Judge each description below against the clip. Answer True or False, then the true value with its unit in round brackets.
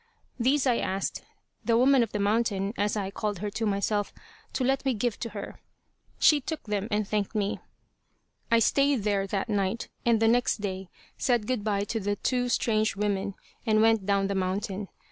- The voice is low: False (210 Hz)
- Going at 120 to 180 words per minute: False (190 wpm)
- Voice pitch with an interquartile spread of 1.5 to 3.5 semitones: True (2.8 semitones)